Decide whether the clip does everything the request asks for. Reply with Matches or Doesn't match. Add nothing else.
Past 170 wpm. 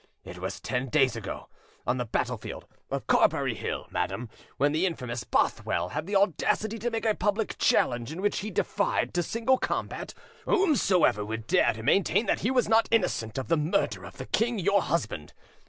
Matches